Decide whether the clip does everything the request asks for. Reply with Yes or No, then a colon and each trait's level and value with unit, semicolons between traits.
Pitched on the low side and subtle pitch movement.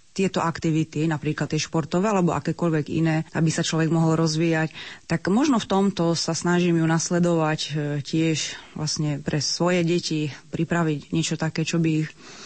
No: medium, 160 Hz; narrow, 1.6 semitones